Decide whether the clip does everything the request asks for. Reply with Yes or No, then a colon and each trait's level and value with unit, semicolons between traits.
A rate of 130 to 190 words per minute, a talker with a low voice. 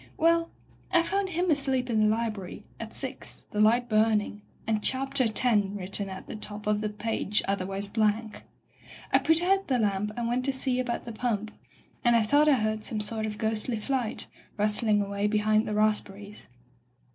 No: average, 185 wpm; high, 220 Hz